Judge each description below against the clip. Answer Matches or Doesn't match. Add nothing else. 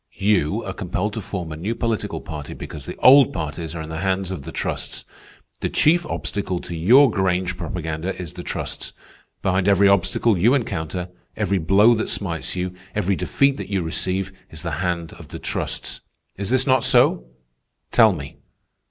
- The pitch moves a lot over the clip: Doesn't match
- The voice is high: Doesn't match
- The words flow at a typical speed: Matches